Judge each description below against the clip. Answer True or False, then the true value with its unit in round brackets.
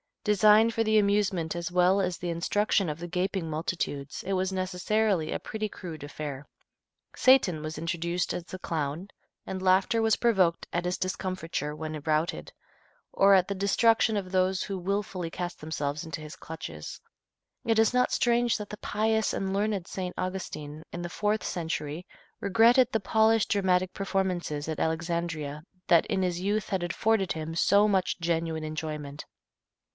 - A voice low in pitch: False (185 Hz)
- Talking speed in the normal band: True (160 wpm)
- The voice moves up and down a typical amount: True (3.9 semitones)